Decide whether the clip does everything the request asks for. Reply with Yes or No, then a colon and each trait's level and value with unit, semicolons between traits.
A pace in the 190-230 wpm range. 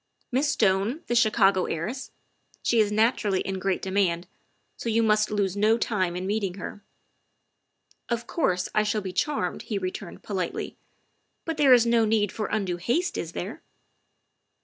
Yes: average, 200 wpm